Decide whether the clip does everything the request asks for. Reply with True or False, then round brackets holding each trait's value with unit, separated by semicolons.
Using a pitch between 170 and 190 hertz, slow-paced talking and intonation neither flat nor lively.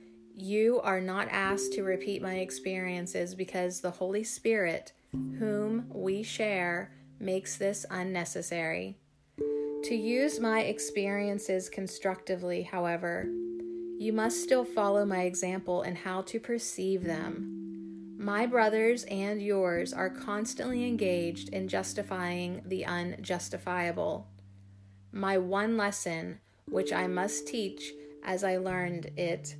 True (185 Hz; 115 wpm; 3.2 semitones)